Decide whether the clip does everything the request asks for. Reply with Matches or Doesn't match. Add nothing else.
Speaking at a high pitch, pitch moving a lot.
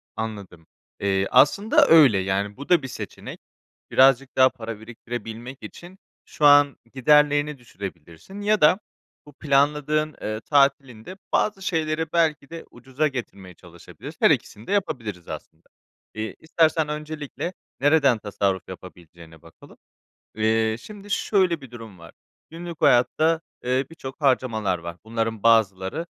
Doesn't match